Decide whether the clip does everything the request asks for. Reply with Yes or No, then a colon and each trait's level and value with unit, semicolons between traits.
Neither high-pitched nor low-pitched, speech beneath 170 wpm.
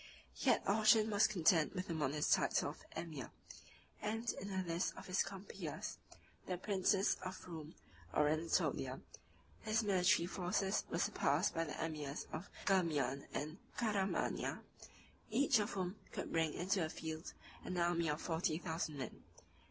Yes: medium, 180 Hz; average, 150 wpm